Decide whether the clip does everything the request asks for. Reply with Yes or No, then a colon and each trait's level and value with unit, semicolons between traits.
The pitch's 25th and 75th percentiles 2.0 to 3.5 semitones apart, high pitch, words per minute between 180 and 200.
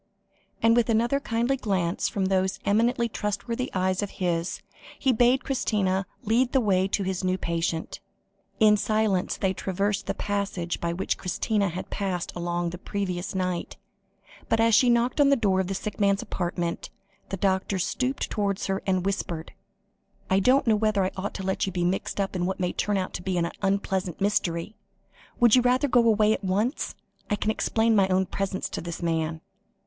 Yes: average, 3.1 semitones; high, 195 Hz; average, 185 wpm